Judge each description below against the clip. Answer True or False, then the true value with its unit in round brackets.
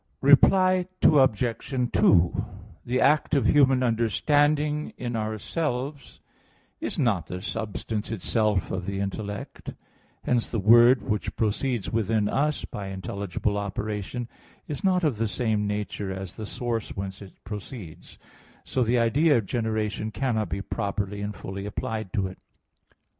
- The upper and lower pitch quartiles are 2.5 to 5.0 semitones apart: True (4.0 semitones)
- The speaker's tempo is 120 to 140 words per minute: True (135 wpm)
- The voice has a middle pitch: False (110 Hz)